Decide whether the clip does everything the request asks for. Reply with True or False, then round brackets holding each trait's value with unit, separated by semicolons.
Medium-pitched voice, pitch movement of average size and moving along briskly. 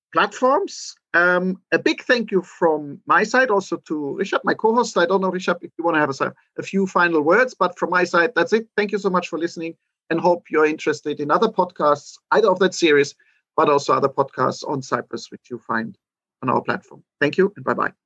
True (175 Hz; 3.8 semitones; 230 wpm)